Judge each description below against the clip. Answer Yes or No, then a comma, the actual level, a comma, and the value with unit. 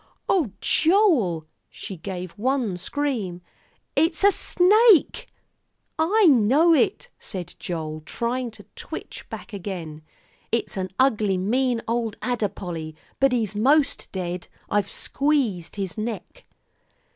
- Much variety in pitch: Yes, wide, 7.6 semitones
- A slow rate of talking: Yes, slow, 120 wpm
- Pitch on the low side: No, high, 225 Hz